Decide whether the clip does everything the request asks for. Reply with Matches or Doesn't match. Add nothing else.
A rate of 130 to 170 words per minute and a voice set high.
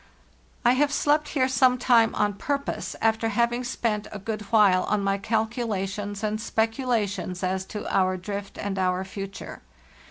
Matches